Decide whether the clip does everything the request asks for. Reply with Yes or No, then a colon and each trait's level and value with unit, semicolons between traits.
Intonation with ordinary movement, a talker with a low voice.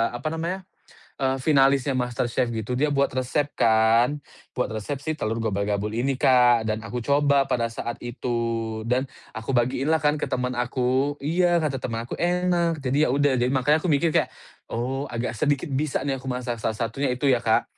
Yes: average, 3.4 semitones; low, 130 Hz